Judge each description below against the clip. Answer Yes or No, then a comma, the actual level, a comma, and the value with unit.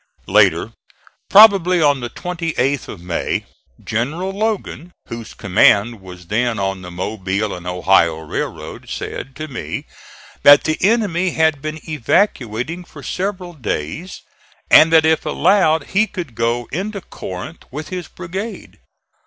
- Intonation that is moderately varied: No, wide, 8.7 semitones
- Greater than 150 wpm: No, slow, 135 wpm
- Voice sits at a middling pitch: Yes, medium, 150 Hz